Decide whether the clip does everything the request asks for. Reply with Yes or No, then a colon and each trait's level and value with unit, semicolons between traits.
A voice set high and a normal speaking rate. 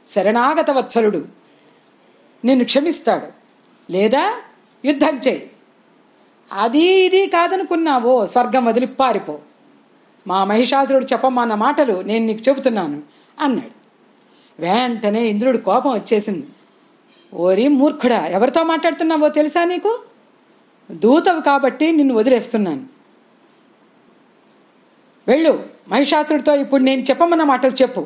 Yes: very high, 265 Hz; average, 90 wpm